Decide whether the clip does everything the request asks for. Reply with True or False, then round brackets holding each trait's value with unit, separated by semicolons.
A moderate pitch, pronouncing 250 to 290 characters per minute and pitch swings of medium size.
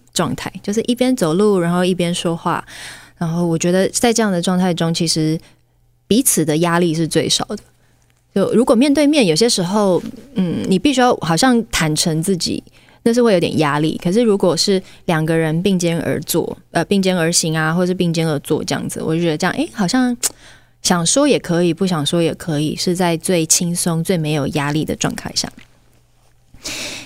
True (175 Hz; 280 characters per minute; 4.1 semitones)